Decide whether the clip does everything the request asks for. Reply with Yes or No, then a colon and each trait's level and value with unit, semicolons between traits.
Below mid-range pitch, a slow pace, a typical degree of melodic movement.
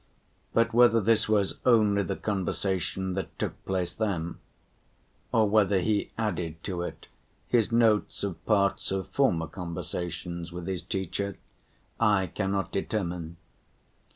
Yes: very low, 95 Hz; slow, 125 wpm; average, 3.5 semitones